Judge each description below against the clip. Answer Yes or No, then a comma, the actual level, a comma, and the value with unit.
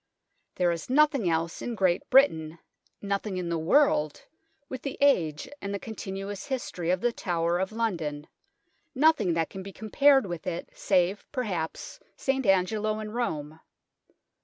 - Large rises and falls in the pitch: Yes, wide, 5.7 semitones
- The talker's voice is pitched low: No, high, 195 Hz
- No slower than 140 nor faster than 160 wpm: Yes, average, 150 wpm